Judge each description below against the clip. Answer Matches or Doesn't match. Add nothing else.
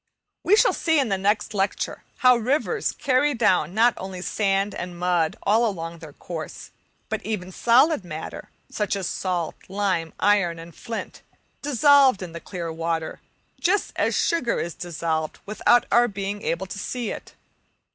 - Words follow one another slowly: Doesn't match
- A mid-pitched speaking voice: Doesn't match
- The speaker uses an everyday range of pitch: Doesn't match